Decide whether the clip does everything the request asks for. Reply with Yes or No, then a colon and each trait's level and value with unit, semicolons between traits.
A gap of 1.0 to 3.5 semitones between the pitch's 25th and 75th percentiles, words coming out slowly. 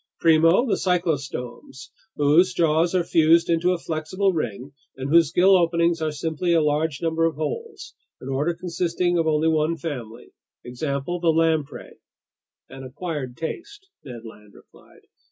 No: average, 3.2 semitones; average, 150 wpm